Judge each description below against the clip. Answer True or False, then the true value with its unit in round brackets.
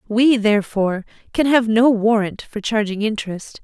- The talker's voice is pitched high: True (220 Hz)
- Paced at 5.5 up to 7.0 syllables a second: False (5.1 syllables/s)